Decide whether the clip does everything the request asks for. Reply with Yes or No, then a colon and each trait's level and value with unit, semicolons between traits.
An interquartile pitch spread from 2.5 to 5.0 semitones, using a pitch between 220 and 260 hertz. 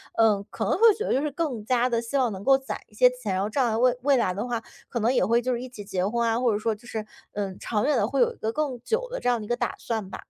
Yes: average, 3.1 semitones; high, 235 Hz